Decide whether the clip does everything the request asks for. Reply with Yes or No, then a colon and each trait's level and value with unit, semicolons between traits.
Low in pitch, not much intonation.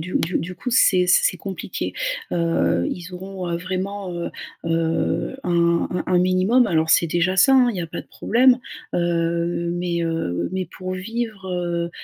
No: medium, 180 Hz; narrow, 1.8 semitones